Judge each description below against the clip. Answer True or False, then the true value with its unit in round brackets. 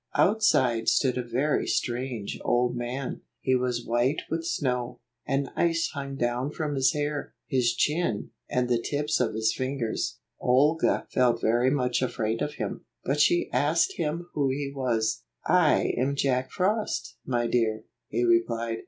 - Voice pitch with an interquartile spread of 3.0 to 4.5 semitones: True (3.3 semitones)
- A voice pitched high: False (130 Hz)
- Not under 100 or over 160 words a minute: True (155 wpm)